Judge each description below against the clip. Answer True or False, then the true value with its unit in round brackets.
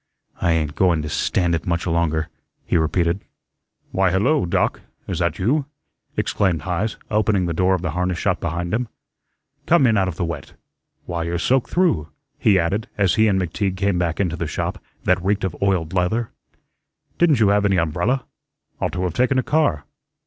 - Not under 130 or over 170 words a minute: False (190 wpm)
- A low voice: True (90 Hz)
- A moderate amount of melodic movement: True (3.5 semitones)